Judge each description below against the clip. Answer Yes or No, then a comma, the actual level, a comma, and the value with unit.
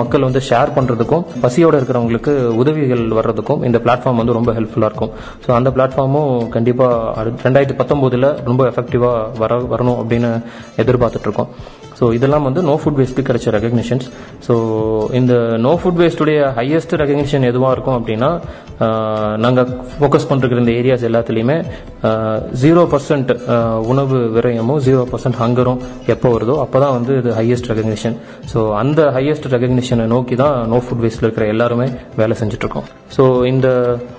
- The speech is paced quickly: Yes, fast, 140 wpm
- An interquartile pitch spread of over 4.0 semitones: No, narrow, 2.4 semitones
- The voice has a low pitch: Yes, low, 125 Hz